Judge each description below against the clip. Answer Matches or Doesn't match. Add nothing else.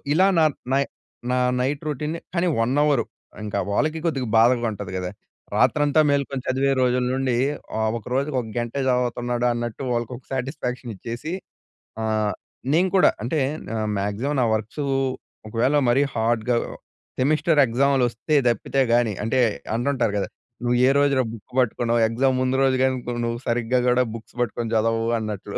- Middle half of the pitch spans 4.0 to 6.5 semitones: Doesn't match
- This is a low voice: Matches